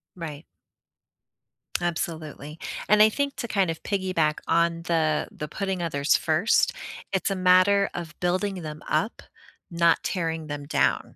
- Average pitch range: Yes, average, 3.5 semitones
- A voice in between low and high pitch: Yes, medium, 170 Hz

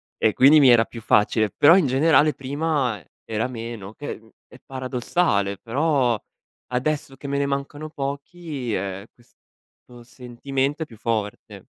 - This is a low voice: Yes, low, 130 Hz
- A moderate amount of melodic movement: Yes, average, 4.1 semitones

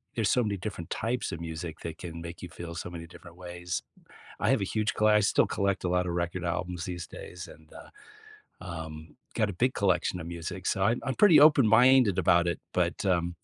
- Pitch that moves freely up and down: No, average, 3.7 semitones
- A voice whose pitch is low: Yes, very low, 90 Hz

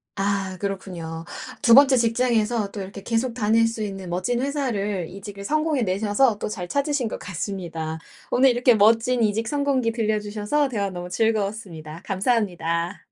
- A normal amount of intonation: Yes, average, 3.8 semitones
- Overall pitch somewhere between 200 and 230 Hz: Yes, high, 210 Hz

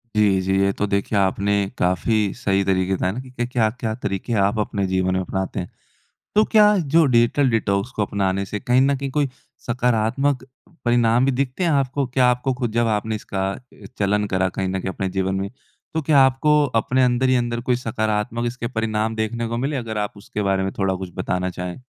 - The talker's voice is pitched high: No, low, 110 Hz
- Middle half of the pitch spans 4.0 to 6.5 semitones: Yes, average, 4.4 semitones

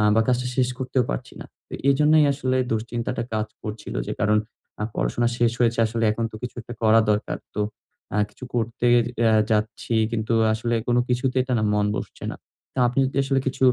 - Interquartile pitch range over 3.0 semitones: No, average, 2.7 semitones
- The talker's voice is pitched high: No, low, 120 Hz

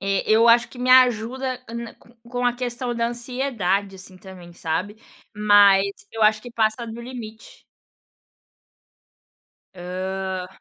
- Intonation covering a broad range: No, average, 3.9 semitones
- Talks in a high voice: Yes, high, 220 Hz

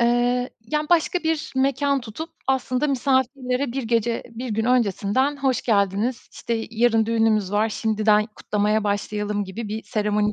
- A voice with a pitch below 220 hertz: No, high, 230 Hz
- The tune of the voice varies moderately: Yes, average, 3.6 semitones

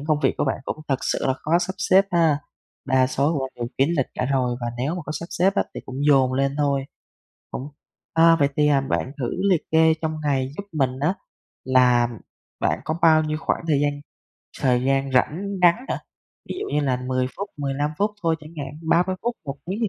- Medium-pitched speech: Yes, medium, 145 Hz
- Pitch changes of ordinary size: Yes, average, 3.7 semitones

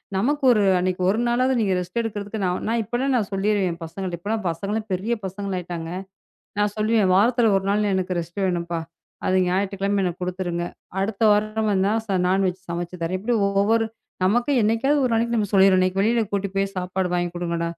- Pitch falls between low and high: No, high, 195 Hz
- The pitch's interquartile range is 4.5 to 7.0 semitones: No, average, 3.2 semitones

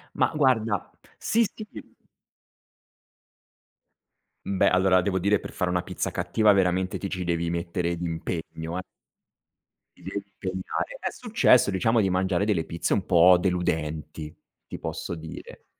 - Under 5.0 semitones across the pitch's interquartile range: Yes, average, 2.7 semitones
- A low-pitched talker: Yes, very low, 90 Hz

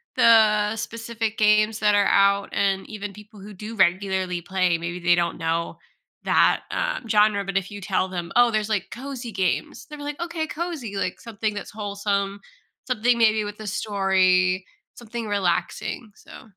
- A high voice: Yes, high, 205 Hz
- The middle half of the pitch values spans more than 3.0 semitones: No, average, 2.7 semitones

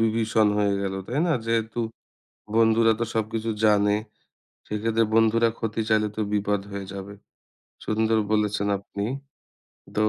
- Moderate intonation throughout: No, narrow, 1.6 semitones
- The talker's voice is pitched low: Yes, low, 110 Hz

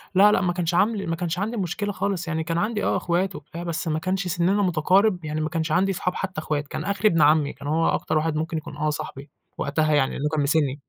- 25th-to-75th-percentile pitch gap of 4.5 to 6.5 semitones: No, average, 3.6 semitones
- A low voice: No, medium, 165 Hz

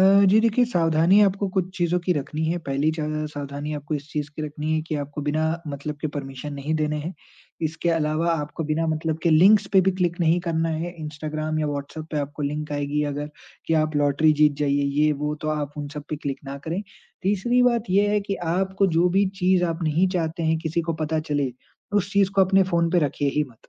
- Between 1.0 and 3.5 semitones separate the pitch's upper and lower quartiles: Yes, average, 3.2 semitones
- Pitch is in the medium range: Yes, medium, 155 Hz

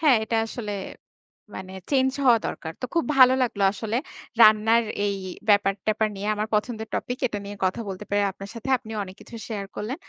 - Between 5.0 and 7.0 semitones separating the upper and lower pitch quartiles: No, average, 2.7 semitones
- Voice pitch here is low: No, high, 215 Hz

